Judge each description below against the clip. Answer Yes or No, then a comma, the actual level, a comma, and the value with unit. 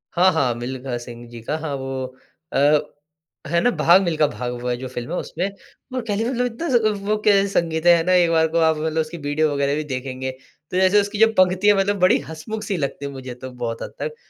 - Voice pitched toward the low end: No, medium, 160 Hz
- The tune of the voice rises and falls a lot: Yes, wide, 6.1 semitones